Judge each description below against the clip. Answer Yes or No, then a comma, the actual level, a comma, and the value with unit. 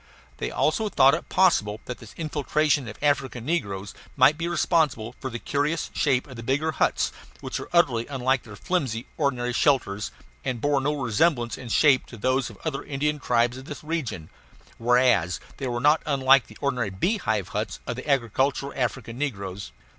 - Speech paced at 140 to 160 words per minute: No, average, 180 wpm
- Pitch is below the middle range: Yes, low, 130 Hz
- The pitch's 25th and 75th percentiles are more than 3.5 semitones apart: Yes, average, 4.1 semitones